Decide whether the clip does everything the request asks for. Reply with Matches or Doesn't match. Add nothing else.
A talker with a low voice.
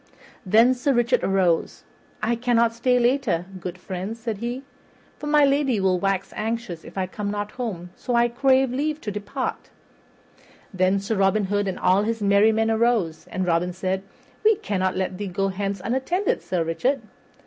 Doesn't match